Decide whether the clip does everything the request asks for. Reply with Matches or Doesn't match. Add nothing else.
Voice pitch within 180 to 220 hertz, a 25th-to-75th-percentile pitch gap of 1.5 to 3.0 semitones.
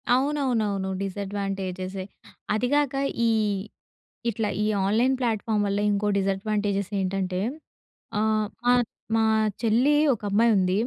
Matches